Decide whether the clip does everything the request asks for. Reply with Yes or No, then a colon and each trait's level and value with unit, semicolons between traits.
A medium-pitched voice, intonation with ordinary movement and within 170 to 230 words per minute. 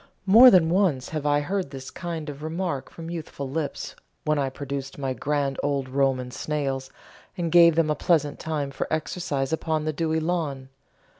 Yes: medium, 150 Hz; average, 3.2 semitones; average, 175 wpm